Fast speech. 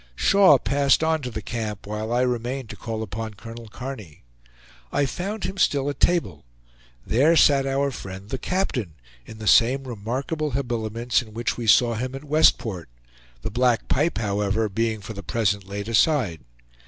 No: average, 170 wpm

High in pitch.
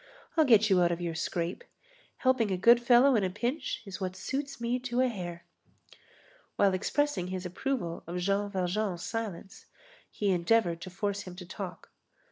Yes: high, 200 Hz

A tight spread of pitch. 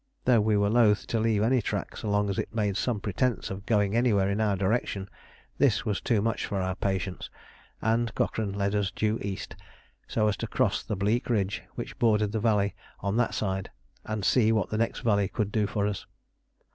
Yes: narrow, 2.1 semitones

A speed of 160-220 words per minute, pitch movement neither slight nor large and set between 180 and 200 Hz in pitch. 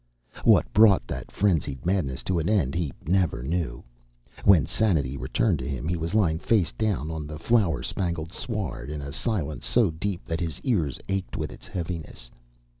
No: average, 180 wpm; average, 4.7 semitones; very low, 85 Hz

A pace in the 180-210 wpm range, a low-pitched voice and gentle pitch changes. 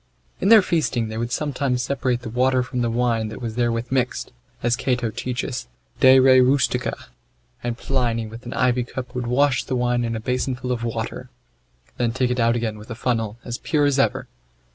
Yes: average, 200 wpm; low, 125 Hz; narrow, 1.8 semitones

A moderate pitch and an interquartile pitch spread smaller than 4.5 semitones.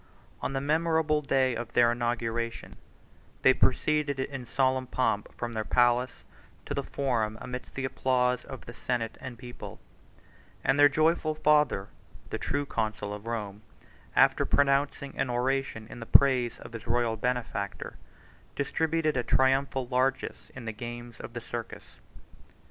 No: low, 125 Hz; average, 2.8 semitones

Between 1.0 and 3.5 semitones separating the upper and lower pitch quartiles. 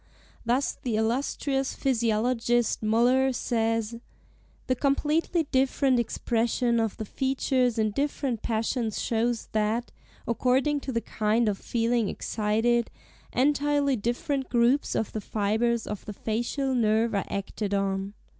Yes: average, 3.1 semitones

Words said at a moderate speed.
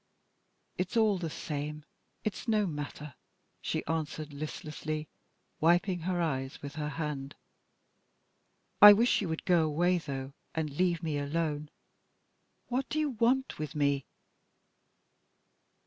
No: slow, 125 wpm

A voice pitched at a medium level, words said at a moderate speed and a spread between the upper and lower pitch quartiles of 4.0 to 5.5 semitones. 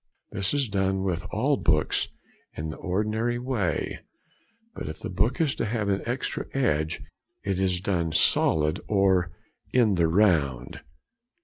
No: very low, 95 Hz; average, 145 wpm; average, 4.7 semitones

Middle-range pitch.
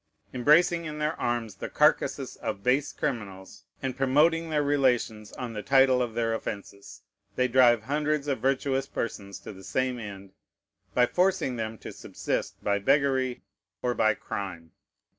No: low, 125 Hz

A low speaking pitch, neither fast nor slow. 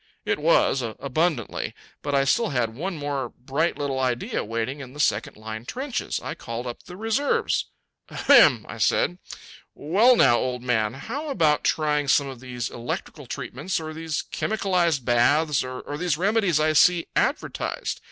No: medium, 145 Hz; average, 160 wpm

